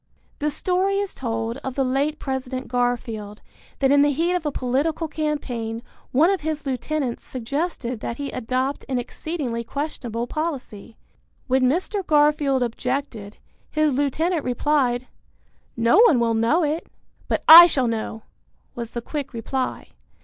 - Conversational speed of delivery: Yes, average, 145 wpm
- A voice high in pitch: Yes, very high, 270 Hz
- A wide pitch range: No, average, 4.2 semitones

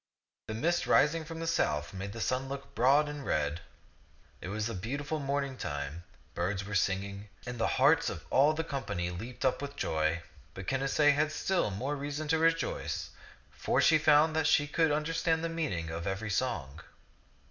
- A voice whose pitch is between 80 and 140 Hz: Yes, low, 135 Hz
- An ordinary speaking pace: Yes, average, 180 wpm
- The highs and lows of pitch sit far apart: Yes, wide, 7.8 semitones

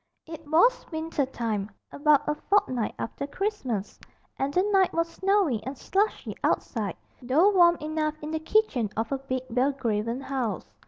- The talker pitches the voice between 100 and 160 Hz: No, very high, 290 Hz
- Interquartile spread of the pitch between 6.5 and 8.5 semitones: No, wide, 5.5 semitones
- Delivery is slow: No, average, 155 wpm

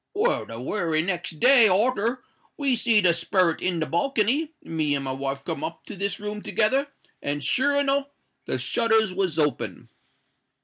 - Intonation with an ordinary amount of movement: No, wide, 7.4 semitones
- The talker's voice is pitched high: Yes, high, 200 Hz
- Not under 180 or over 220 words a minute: No, average, 170 wpm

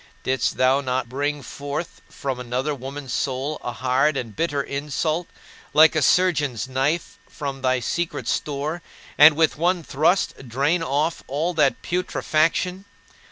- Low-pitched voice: No, medium, 145 Hz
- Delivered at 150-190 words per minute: No, average, 140 wpm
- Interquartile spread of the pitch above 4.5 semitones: No, average, 3.3 semitones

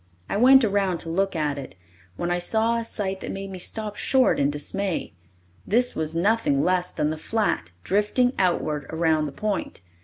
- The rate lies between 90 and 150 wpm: No, average, 185 wpm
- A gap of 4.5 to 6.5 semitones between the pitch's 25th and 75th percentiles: Yes, average, 5.1 semitones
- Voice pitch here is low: No, high, 190 Hz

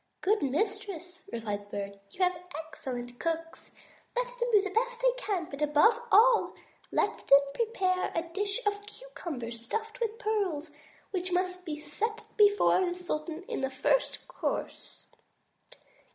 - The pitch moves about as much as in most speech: No, wide, 6.2 semitones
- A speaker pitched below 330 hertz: No, very high, 365 Hz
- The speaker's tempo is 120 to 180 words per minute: Yes, average, 150 wpm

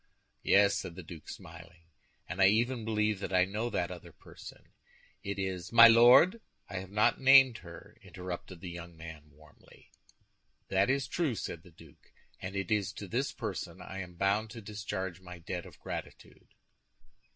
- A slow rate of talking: No, average, 175 wpm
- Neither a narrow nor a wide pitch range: Yes, average, 3.8 semitones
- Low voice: Yes, very low, 95 Hz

